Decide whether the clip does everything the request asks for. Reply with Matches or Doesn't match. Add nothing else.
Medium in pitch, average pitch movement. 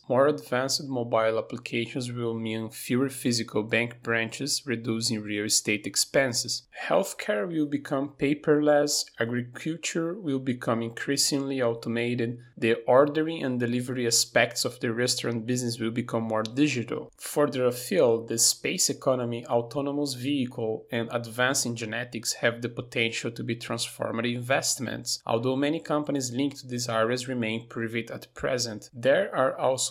Doesn't match